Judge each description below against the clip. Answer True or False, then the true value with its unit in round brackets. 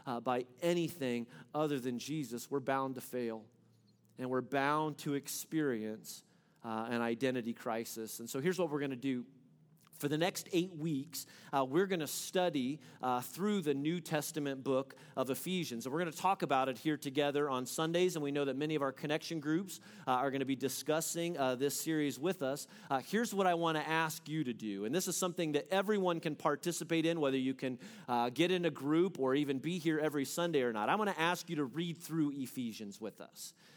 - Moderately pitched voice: True (150 Hz)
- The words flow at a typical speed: False (215 wpm)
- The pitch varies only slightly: False (4.3 semitones)